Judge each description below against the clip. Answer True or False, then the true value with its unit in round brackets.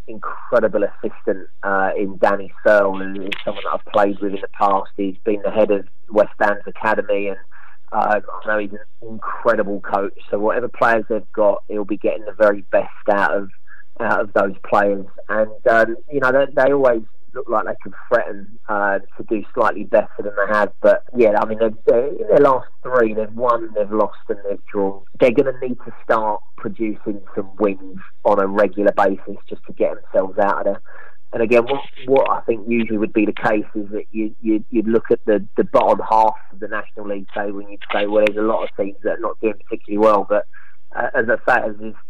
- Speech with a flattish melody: True (2.0 semitones)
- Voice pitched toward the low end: True (105 Hz)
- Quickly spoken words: True (220 wpm)